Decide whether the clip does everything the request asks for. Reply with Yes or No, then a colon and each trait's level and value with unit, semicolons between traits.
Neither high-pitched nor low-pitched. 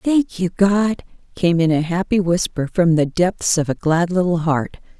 Yes: medium, 175 Hz